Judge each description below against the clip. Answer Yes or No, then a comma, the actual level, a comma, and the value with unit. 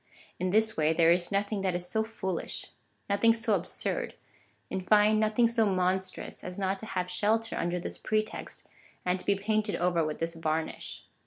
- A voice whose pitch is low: No, high, 190 Hz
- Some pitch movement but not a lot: Yes, average, 3.3 semitones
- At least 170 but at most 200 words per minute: Yes, average, 185 wpm